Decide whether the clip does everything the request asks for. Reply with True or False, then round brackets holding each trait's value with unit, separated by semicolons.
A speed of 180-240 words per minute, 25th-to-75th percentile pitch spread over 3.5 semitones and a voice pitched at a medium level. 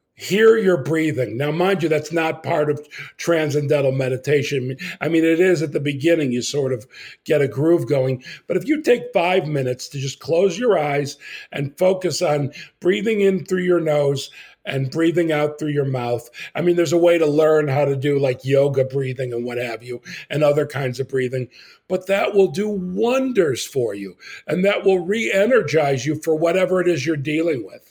True (200 wpm; 4.5 semitones; 150 Hz)